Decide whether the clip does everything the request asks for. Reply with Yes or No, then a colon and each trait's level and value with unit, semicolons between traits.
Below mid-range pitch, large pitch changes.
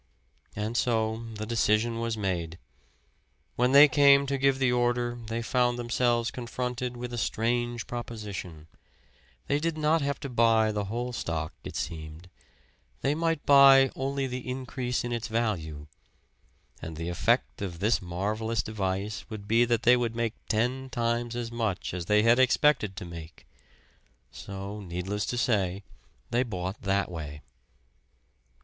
No: low, 115 Hz; average, 3.9 semitones